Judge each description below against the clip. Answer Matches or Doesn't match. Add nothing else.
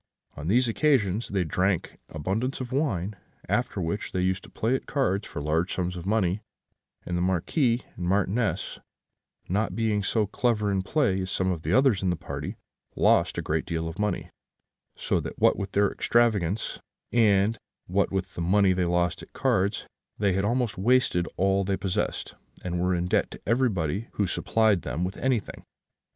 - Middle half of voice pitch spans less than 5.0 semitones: Matches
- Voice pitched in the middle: Doesn't match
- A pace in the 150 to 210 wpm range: Matches